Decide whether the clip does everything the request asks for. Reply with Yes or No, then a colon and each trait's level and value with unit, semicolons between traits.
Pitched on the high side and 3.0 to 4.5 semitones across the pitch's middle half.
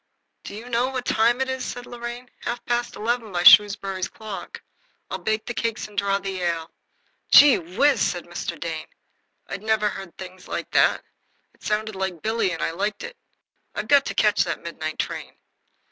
Yes: high, 215 Hz; average, 4.2 semitones